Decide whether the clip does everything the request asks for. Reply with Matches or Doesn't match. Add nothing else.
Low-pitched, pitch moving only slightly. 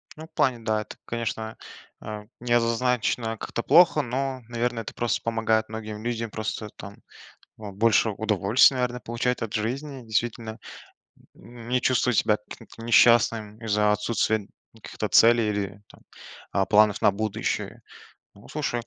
Matches